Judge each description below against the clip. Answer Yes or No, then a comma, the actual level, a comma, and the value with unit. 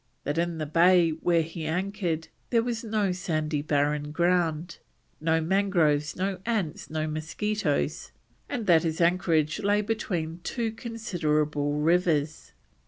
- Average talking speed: No, slow, 130 wpm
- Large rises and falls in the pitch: No, average, 4.1 semitones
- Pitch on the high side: No, medium, 170 Hz